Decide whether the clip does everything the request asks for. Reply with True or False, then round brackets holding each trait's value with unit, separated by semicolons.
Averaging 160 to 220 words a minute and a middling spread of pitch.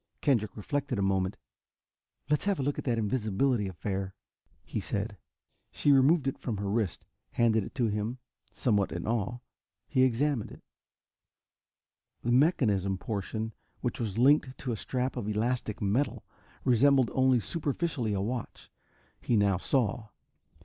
False (145 wpm; 4.3 semitones)